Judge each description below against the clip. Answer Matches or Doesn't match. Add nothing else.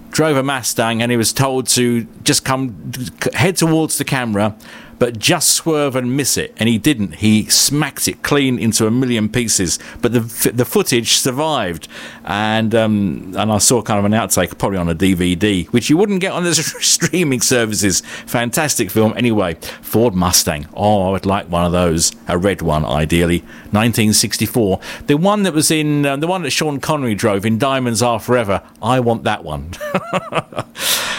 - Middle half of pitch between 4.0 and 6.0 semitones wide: Matches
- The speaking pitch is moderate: Doesn't match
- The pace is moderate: Matches